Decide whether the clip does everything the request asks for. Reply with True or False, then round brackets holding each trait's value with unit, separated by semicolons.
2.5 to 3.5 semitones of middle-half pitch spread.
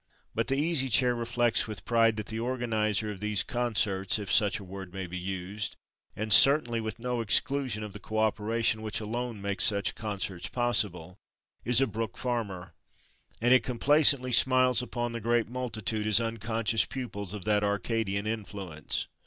True (3.0 semitones)